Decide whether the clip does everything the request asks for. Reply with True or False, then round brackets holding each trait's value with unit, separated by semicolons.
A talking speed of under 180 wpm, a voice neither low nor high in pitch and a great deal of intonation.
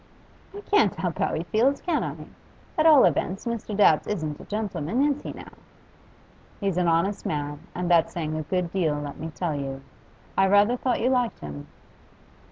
False (185 wpm; 180 Hz; 6.1 semitones)